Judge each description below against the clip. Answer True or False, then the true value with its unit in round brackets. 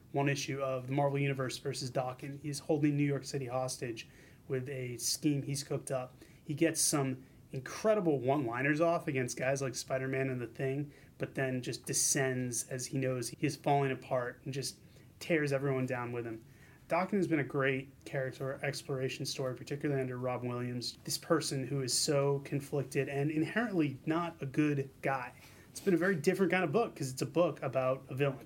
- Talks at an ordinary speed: True (190 wpm)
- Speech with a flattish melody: True (2.3 semitones)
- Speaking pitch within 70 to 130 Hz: False (140 Hz)